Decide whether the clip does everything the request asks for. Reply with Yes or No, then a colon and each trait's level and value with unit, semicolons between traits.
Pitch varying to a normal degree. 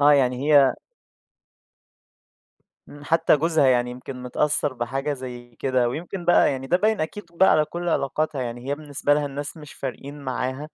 Yes: average, 3.2 semitones